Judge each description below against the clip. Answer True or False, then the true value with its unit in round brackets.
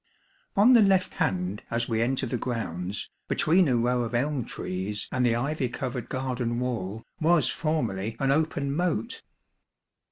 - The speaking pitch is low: True (125 Hz)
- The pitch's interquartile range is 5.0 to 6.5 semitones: False (4.5 semitones)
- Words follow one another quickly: False (155 wpm)